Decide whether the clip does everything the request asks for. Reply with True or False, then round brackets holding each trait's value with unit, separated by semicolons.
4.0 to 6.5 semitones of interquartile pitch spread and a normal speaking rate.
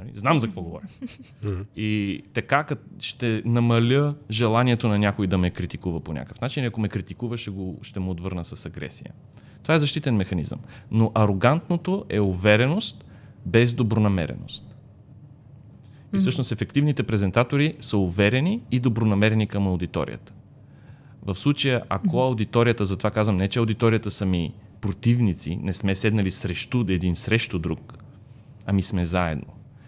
True (4.5 semitones; 140 wpm)